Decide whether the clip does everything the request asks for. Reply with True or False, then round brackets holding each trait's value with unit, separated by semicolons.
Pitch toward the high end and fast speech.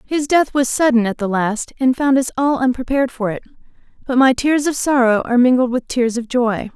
True (255 Hz; 220 wpm)